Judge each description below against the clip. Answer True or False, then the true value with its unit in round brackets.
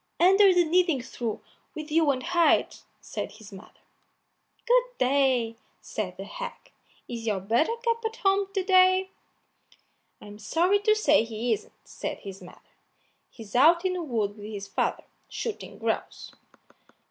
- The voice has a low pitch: False (320 Hz)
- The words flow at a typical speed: True (145 wpm)